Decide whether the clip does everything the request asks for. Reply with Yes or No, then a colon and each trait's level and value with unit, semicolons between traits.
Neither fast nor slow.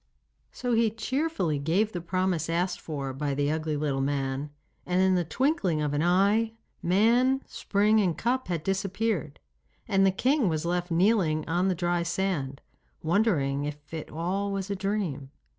Yes: average, 165 wpm